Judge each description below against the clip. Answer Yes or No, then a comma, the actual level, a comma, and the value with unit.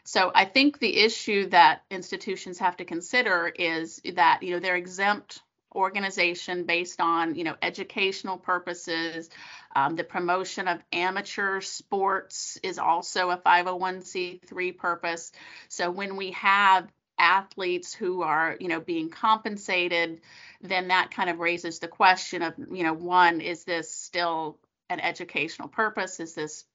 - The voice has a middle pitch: Yes, medium, 180 Hz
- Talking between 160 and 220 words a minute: No, average, 145 wpm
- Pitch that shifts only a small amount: Yes, narrow, 2.0 semitones